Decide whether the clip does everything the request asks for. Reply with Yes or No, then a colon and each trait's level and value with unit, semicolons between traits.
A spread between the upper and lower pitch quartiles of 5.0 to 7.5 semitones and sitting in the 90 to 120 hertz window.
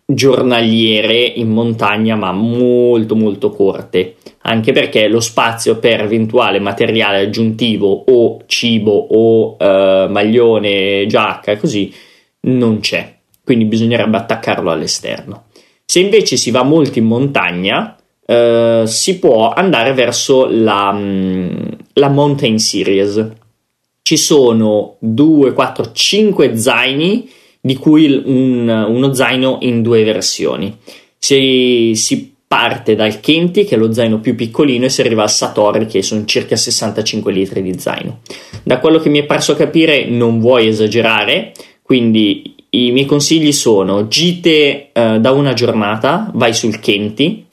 No: average, 3.5 semitones; low, 115 Hz